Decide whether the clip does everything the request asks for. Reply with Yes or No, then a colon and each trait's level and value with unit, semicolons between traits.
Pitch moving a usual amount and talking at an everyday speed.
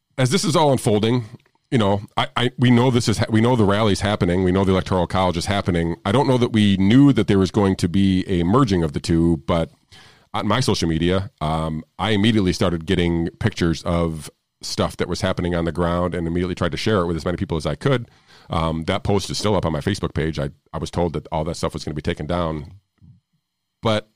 No: average, 4.2 semitones; fast, 250 wpm